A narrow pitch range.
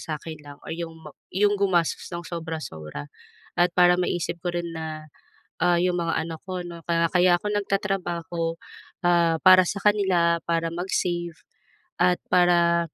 Yes: narrow, 1.5 semitones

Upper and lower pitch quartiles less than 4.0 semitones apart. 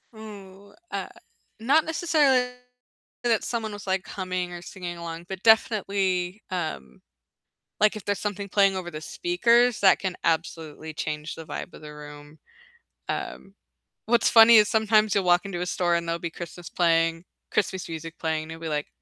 No: average, 4.4 semitones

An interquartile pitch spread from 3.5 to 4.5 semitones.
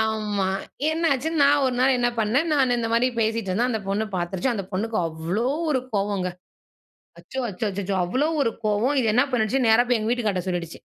Yes: average, 4.2 semitones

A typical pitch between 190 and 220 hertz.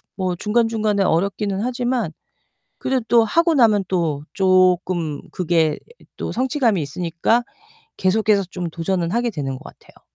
Yes: high, 195 Hz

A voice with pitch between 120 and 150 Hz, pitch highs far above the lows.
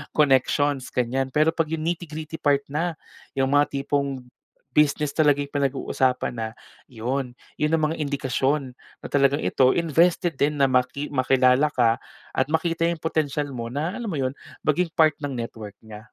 No: medium, 140 Hz; average, 3.0 semitones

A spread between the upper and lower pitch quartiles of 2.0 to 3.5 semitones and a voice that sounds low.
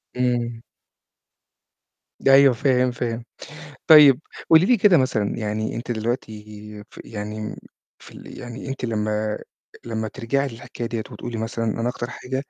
Yes: average, 3.0 semitones; low, 120 Hz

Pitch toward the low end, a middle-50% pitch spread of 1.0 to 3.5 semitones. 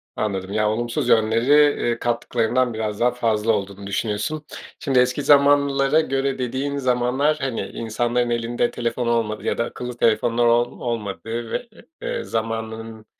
Yes: low, 120 Hz; narrow, 2.5 semitones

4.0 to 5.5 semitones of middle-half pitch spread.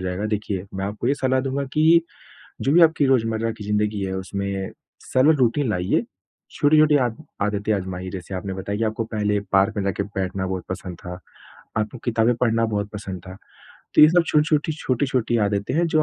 Yes: average, 5.2 semitones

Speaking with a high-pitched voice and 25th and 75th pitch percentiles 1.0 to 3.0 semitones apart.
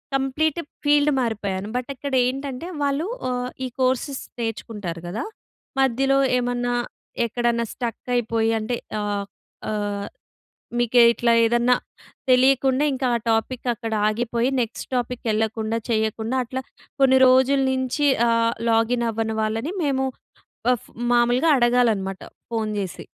Yes: high, 240 Hz; average, 2.7 semitones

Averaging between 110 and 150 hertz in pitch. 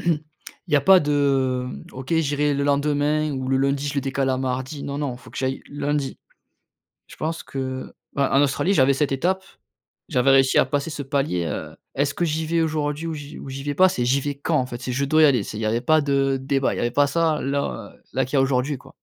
Yes: medium, 140 Hz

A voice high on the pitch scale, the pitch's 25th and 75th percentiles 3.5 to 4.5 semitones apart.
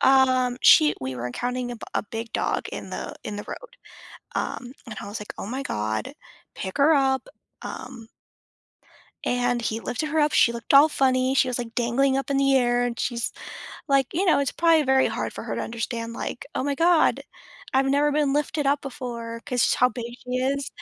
No: very high, 255 Hz; average, 2.9 semitones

